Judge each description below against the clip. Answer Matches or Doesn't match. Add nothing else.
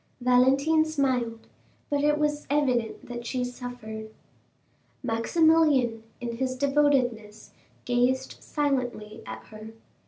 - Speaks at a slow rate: Matches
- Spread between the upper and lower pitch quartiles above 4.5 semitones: Doesn't match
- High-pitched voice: Matches